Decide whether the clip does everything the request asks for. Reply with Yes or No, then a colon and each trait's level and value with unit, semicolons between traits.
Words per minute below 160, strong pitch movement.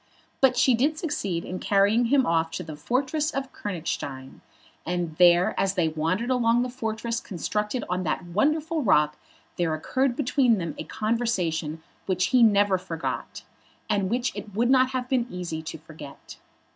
No: average, 165 wpm; wide, 6.8 semitones